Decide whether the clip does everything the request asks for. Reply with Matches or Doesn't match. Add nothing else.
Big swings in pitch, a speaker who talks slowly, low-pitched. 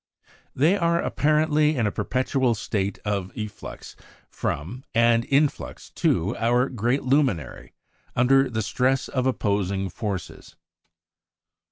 Doesn't match